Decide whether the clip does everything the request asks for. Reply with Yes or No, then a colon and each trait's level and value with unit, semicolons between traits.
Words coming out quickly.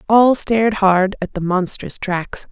No: average, 165 wpm